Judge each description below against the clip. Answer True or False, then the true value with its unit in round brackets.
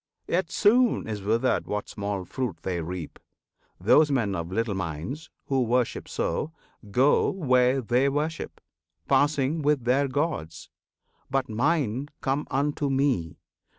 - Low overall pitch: True (130 Hz)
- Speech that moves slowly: True (130 wpm)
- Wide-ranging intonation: True (5.8 semitones)